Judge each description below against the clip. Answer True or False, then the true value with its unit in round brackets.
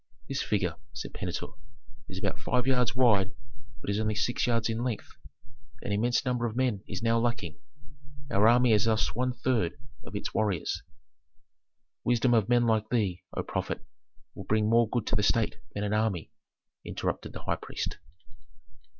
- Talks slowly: False (170 wpm)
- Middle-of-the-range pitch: False (115 Hz)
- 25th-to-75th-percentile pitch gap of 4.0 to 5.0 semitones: False (2.7 semitones)